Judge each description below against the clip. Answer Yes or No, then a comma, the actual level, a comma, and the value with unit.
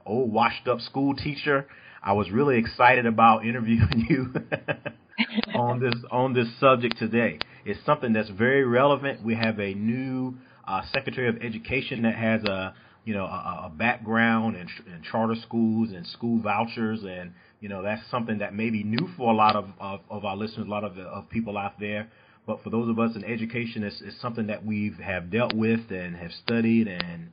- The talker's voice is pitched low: Yes, low, 115 Hz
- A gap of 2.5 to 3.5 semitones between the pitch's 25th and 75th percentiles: Yes, average, 2.8 semitones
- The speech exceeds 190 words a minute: Yes, average, 200 wpm